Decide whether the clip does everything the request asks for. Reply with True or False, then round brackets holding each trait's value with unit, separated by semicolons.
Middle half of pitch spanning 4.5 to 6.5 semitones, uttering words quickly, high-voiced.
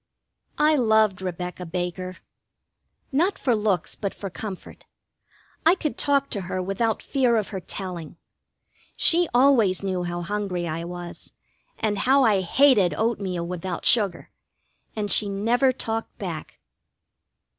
False (4.9 semitones; 135 wpm; 200 Hz)